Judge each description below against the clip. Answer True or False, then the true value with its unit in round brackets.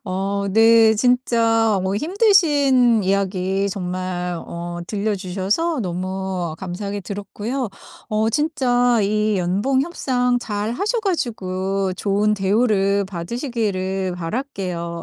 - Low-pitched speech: False (205 Hz)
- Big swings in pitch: False (4.5 semitones)